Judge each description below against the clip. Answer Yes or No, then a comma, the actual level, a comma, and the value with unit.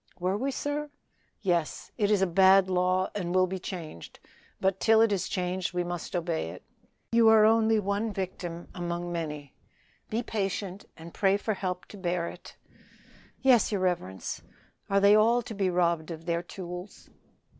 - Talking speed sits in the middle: Yes, average, 170 wpm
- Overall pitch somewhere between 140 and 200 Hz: Yes, medium, 185 Hz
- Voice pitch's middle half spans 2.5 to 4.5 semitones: Yes, average, 3.1 semitones